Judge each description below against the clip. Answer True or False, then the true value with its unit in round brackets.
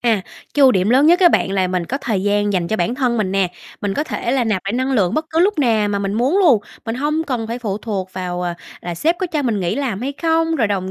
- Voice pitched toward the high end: True (225 Hz)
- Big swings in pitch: True (6.2 semitones)